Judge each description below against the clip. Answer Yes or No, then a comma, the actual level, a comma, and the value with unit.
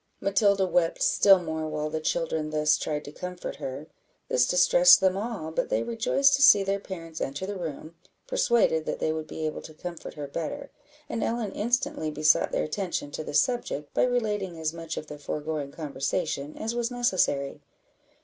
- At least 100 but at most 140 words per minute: No, average, 185 wpm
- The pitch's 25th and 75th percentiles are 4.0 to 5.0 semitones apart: Yes, average, 4.6 semitones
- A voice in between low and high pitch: Yes, medium, 165 Hz